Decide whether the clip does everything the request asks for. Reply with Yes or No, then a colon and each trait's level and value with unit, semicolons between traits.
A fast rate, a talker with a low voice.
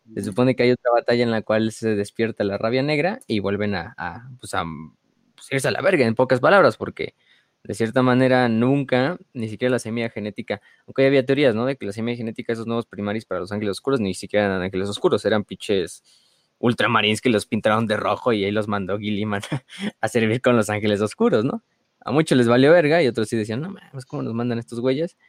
Yes: fast, 230 wpm; low, 115 Hz